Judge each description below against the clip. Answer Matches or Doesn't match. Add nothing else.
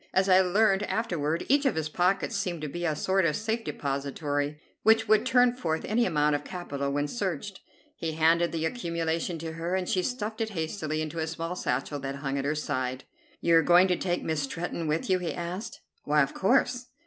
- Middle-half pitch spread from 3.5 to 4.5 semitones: Matches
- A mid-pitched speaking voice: Matches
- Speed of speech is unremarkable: Doesn't match